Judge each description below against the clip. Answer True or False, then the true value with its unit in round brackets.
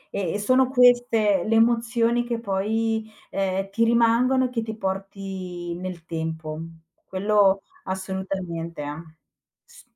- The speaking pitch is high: True (200 Hz)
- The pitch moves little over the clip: False (3.7 semitones)